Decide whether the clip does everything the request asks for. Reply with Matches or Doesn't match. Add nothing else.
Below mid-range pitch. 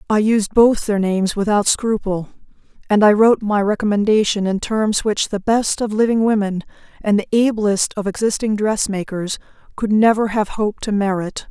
Doesn't match